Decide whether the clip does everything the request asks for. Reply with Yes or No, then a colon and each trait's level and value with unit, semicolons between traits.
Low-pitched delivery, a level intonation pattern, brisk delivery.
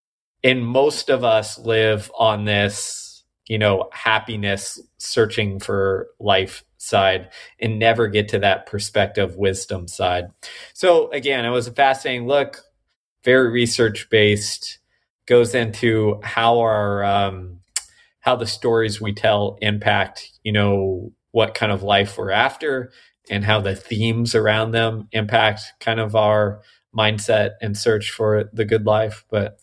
No: low, 110 Hz; narrow, 2.0 semitones; average, 140 wpm